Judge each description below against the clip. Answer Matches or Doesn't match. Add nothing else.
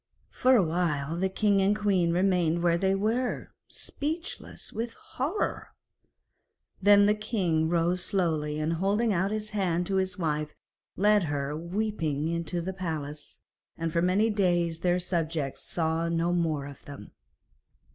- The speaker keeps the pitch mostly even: Doesn't match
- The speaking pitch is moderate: Matches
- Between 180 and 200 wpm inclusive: Doesn't match